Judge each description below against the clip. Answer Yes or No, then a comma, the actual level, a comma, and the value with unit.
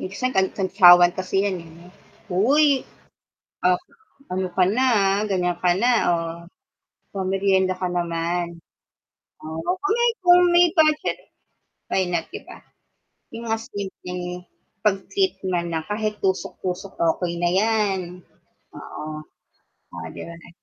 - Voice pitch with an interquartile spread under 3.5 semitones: Yes, average, 3.1 semitones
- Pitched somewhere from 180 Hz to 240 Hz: Yes, high, 190 Hz